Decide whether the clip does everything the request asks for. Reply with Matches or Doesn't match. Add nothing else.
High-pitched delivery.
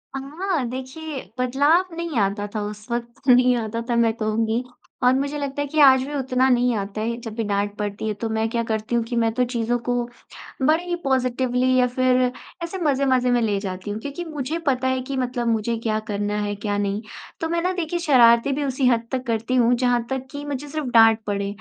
Matches